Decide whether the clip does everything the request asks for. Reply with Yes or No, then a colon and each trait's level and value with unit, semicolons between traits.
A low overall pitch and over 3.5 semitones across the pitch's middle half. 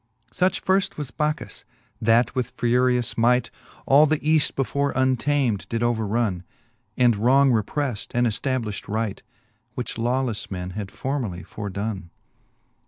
Yes: low, 120 Hz; average, 3.9 semitones